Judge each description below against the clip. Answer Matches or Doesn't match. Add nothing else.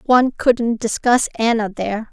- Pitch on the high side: Matches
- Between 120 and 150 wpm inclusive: Matches